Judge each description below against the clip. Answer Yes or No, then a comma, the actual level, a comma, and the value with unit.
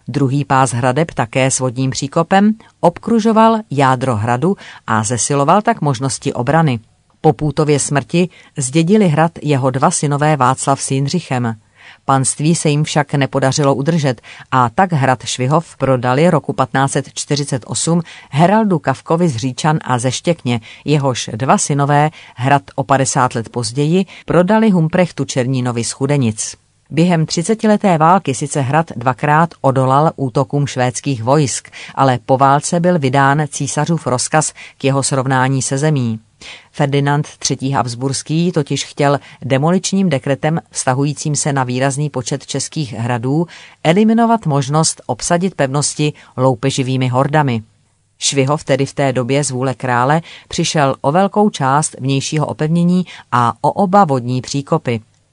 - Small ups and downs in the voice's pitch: No, average, 3.4 semitones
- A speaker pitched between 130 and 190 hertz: Yes, medium, 140 Hz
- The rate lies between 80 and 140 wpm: Yes, average, 130 wpm